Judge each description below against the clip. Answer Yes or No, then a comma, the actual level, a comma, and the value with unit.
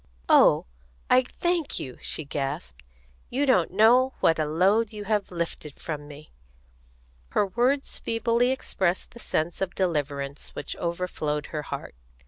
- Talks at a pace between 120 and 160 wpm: Yes, average, 140 wpm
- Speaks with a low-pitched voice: No, medium, 180 Hz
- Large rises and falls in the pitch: Yes, wide, 7.5 semitones